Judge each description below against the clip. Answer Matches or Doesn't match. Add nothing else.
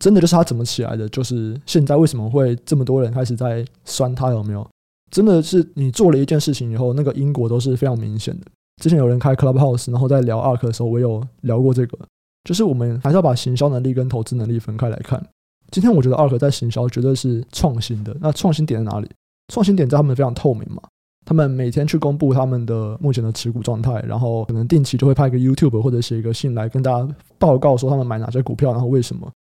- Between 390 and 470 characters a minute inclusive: Matches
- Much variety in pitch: Doesn't match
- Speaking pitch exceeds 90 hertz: Matches